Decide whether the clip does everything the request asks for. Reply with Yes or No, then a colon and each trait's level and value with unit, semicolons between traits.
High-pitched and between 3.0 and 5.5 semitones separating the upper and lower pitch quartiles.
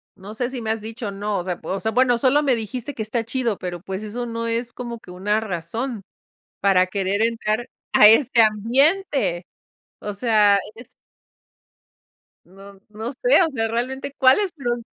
Yes: high, 225 Hz; average, 3.5 semitones